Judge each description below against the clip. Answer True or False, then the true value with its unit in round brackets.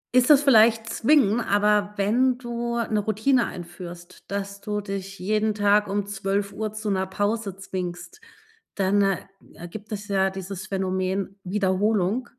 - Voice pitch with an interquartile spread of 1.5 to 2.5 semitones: True (2.1 semitones)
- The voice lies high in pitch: True (205 Hz)